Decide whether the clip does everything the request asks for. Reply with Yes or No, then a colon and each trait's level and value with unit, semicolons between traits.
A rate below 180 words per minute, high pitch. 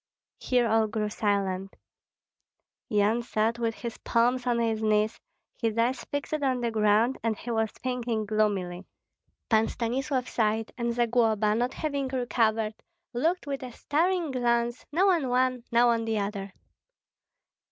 Yes: average, 145 wpm; high, 235 Hz